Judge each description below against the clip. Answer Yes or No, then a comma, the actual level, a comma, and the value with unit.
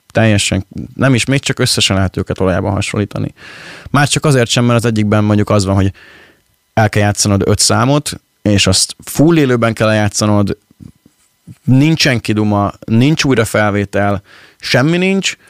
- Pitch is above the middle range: No, low, 110 Hz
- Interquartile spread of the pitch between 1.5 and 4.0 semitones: No, average, 4.7 semitones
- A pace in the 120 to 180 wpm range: Yes, average, 150 wpm